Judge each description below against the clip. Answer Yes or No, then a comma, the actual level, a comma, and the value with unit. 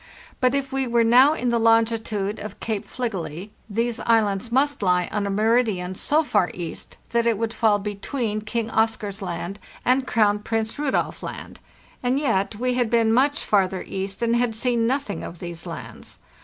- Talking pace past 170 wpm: Yes, average, 180 wpm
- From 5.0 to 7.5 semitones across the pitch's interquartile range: No, average, 3.4 semitones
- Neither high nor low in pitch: No, high, 225 Hz